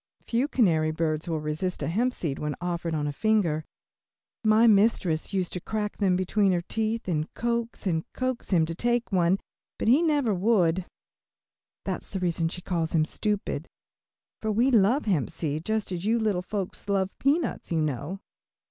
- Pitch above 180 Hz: Yes, high, 190 Hz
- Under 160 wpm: No, average, 175 wpm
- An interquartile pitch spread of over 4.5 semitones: Yes, average, 5.0 semitones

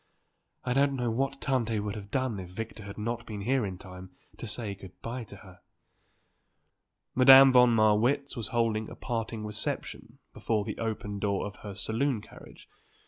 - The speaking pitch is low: Yes, low, 110 Hz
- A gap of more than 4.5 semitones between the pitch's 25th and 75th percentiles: No, average, 3.3 semitones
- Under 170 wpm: No, average, 175 wpm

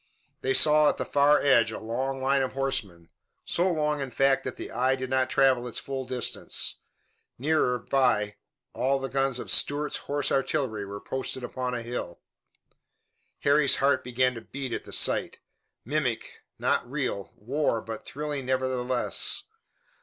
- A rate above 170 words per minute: No, average, 160 wpm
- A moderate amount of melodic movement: No, narrow, 2.2 semitones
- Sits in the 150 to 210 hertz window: No, low, 130 Hz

